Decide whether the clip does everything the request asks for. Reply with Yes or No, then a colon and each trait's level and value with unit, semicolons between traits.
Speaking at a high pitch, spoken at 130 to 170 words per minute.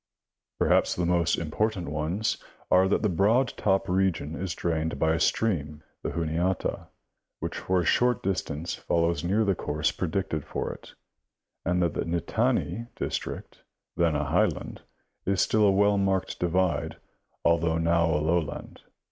No: very low, 85 Hz; average, 150 wpm